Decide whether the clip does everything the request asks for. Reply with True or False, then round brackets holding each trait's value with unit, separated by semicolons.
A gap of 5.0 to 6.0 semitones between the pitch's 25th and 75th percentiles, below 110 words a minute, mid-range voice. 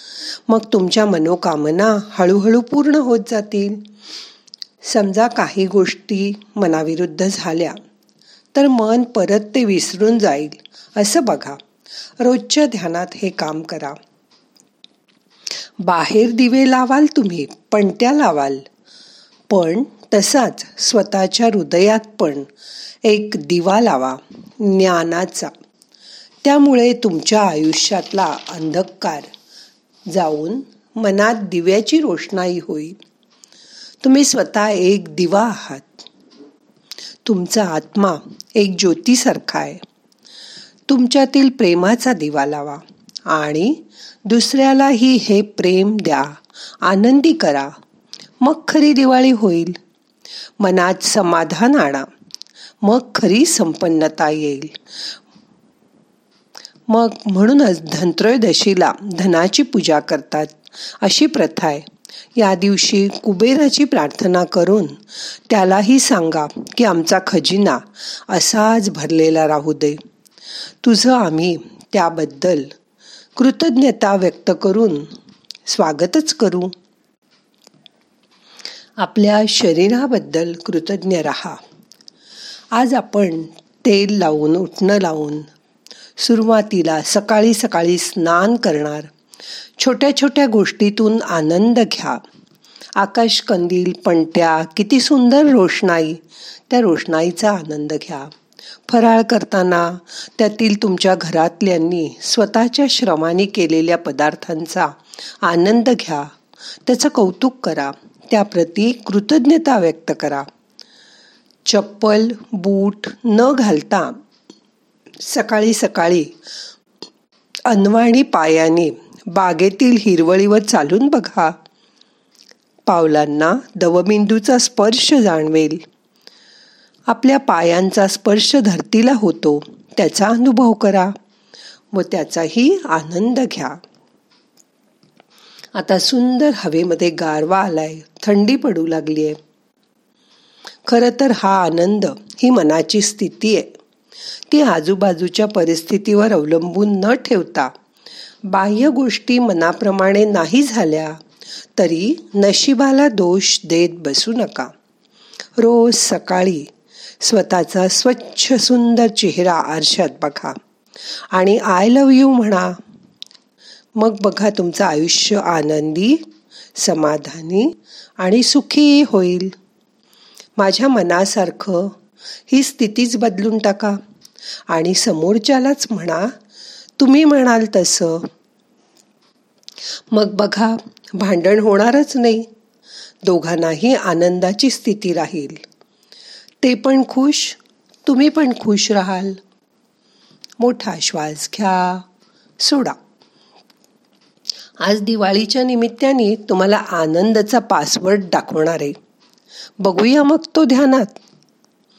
False (5.3 semitones; 85 wpm; 205 Hz)